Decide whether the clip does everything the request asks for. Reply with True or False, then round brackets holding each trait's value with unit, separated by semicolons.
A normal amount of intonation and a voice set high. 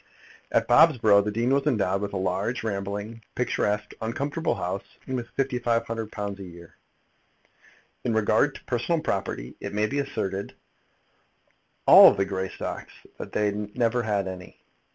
False (3.6 semitones; 105 Hz)